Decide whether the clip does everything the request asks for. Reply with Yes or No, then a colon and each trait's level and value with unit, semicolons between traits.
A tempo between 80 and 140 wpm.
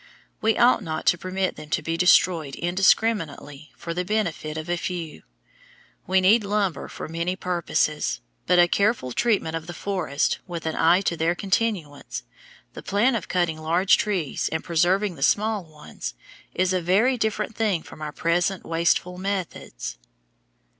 No: average, 160 wpm